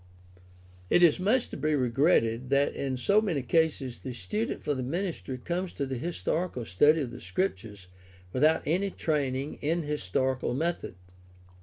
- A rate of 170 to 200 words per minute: No, average, 155 wpm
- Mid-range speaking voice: Yes, medium, 145 Hz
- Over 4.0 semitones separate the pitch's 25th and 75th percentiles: Yes, average, 5.0 semitones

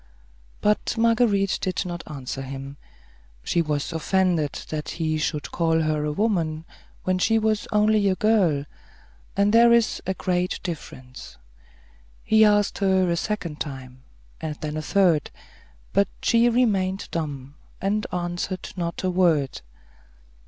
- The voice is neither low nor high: Yes, medium, 180 Hz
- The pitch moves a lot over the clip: No, average, 5.0 semitones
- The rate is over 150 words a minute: No, average, 140 wpm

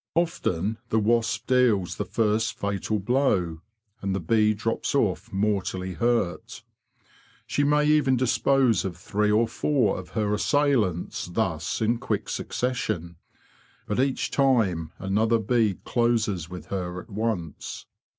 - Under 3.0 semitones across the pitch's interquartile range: No, average, 4.3 semitones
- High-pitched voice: No, low, 110 Hz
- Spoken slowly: Yes, slow, 130 wpm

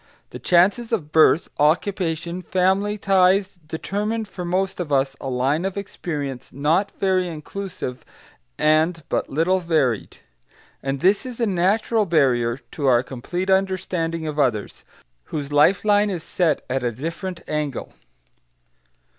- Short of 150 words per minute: Yes, average, 140 wpm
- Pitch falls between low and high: Yes, medium, 170 Hz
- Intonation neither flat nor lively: Yes, average, 4.8 semitones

